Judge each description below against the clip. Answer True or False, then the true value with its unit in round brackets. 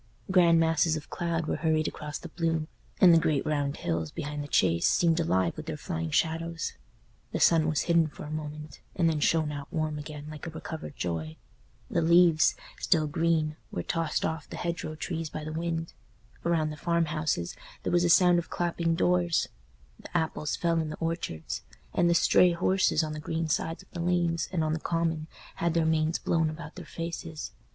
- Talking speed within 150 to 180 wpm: False (195 wpm)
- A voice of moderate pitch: True (160 Hz)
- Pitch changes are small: True (1.7 semitones)